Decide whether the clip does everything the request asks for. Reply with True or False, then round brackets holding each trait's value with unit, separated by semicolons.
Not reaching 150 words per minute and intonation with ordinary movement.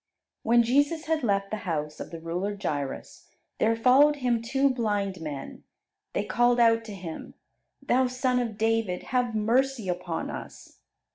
False (155 wpm; 5.0 semitones)